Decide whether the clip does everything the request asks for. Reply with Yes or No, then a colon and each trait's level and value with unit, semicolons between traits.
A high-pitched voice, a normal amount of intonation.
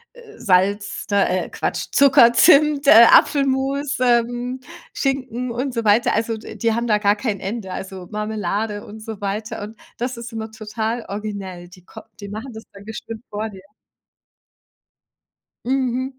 Yes: high, 225 Hz; average, 3.5 semitones